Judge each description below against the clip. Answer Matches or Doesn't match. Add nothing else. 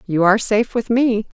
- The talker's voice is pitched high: Matches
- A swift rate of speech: Matches